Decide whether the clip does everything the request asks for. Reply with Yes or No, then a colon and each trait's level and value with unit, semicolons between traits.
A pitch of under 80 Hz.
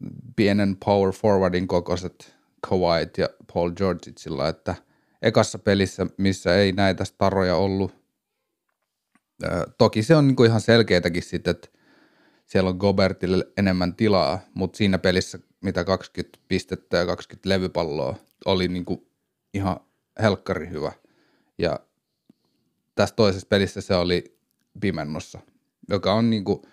No: very low, 95 Hz